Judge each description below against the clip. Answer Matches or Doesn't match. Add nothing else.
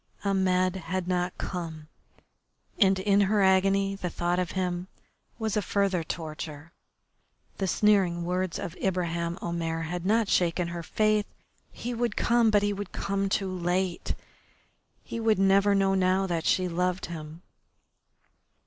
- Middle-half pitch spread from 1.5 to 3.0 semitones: Matches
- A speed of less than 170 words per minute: Matches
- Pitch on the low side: Doesn't match